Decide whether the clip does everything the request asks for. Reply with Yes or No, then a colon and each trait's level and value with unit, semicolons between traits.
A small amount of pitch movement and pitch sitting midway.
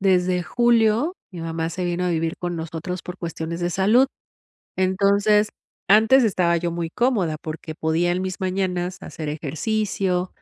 No: average, 3.1 semitones; medium, 180 Hz